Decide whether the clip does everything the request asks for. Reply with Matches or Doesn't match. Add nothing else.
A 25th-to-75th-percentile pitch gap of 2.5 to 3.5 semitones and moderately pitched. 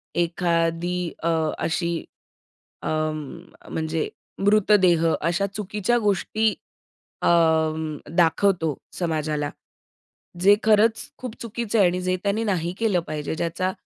Doesn't match